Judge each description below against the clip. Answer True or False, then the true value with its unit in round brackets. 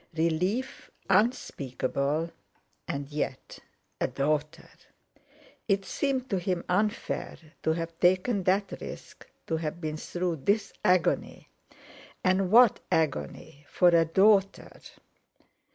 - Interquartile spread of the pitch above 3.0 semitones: True (4.1 semitones)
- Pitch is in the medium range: True (175 Hz)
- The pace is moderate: False (90 wpm)